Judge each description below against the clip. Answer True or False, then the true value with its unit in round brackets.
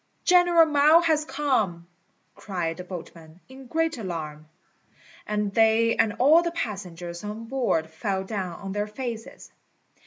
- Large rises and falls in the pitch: True (7.3 semitones)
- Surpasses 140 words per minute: False (135 wpm)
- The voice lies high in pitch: True (215 Hz)